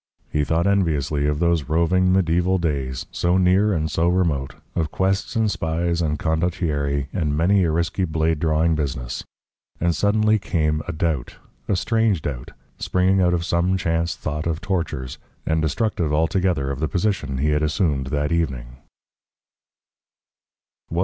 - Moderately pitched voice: No, very low, 80 Hz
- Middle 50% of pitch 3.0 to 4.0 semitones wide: Yes, average, 3.5 semitones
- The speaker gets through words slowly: No, average, 150 wpm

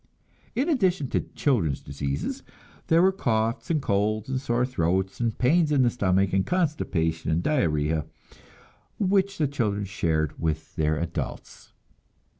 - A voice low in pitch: Yes, low, 110 Hz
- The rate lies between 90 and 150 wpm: Yes, average, 140 wpm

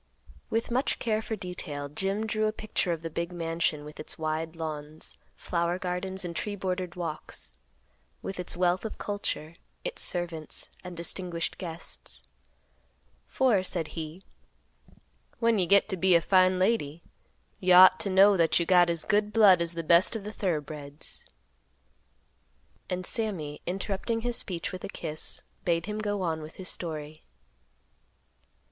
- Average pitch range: Yes, average, 3.3 semitones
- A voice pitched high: No, medium, 180 Hz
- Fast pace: No, average, 160 wpm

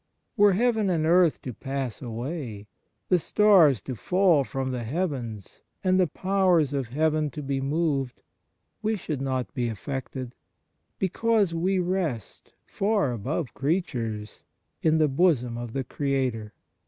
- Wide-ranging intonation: Yes, wide, 6.2 semitones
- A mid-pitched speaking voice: Yes, medium, 145 Hz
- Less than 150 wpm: Yes, average, 140 wpm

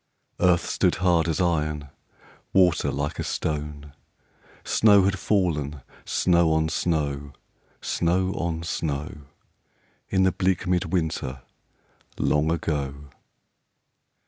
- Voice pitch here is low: Yes, very low, 80 Hz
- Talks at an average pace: No, slow, 105 wpm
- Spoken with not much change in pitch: No, average, 3.6 semitones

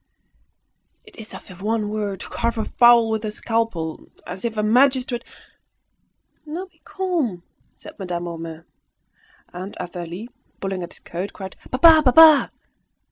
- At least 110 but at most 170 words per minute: Yes, average, 150 wpm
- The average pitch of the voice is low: No, high, 215 Hz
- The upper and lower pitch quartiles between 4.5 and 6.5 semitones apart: Yes, average, 5.0 semitones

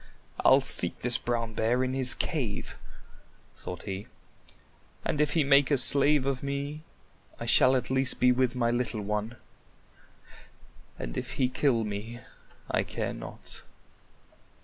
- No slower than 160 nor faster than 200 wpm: No, average, 145 wpm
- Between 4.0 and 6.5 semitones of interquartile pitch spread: No, average, 3.1 semitones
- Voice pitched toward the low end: Yes, low, 125 Hz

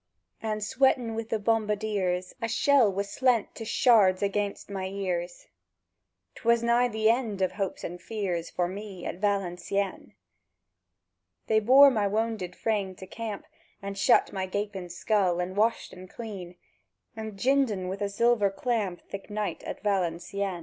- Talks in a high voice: Yes, high, 205 Hz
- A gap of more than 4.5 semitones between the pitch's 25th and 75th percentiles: No, average, 3.1 semitones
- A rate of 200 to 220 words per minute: No, average, 155 wpm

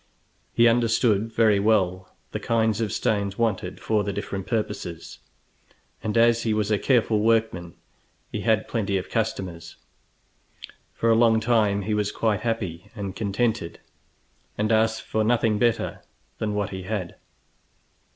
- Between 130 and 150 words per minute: Yes, average, 145 wpm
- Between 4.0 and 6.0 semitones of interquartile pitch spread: No, narrow, 2.4 semitones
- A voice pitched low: Yes, low, 110 Hz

